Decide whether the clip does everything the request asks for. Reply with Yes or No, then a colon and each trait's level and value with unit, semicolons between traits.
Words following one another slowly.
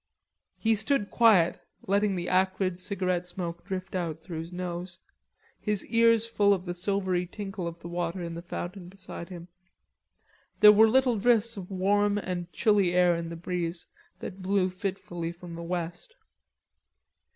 No: average, 160 wpm